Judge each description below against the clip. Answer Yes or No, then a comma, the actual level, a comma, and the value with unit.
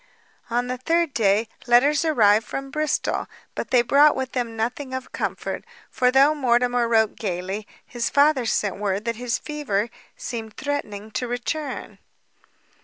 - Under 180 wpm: Yes, average, 150 wpm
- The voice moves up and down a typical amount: Yes, average, 4.0 semitones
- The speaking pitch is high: Yes, high, 245 Hz